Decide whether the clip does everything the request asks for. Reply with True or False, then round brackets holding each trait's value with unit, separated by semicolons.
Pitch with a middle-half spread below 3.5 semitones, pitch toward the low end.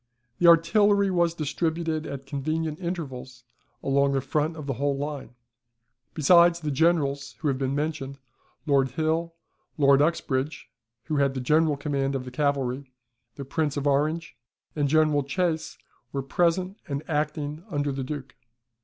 False (2.8 semitones; 150 Hz)